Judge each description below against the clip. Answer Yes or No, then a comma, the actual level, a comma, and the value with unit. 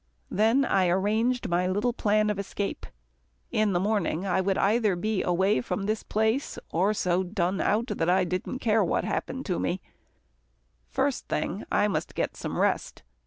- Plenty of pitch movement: No, average, 3.0 semitones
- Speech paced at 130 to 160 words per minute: No, average, 170 wpm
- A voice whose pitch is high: Yes, high, 200 Hz